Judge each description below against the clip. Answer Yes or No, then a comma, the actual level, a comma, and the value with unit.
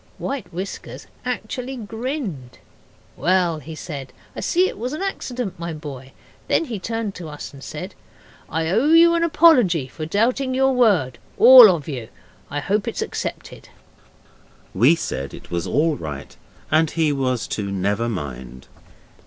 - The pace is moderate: Yes, average, 155 wpm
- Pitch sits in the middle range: Yes, medium, 170 Hz